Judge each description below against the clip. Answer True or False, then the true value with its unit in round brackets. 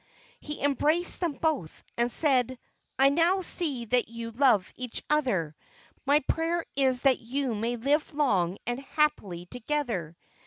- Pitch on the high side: True (260 Hz)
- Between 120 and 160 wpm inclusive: True (145 wpm)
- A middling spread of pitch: True (4.6 semitones)